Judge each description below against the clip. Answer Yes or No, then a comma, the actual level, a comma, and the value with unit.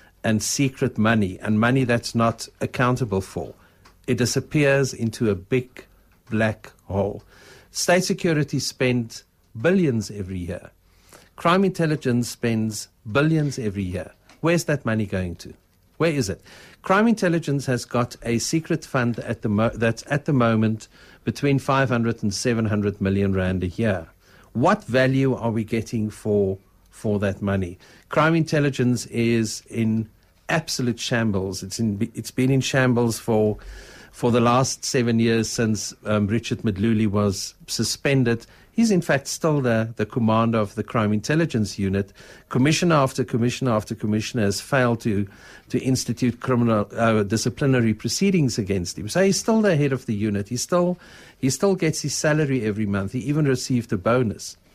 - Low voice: Yes, low, 115 Hz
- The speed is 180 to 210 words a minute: No, average, 155 wpm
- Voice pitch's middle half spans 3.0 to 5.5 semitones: Yes, average, 4.1 semitones